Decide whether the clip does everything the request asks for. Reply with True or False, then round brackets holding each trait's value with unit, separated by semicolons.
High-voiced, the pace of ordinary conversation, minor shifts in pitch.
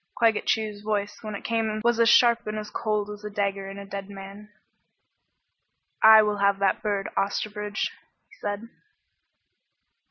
True (210 Hz; 160 wpm; 1.4 semitones)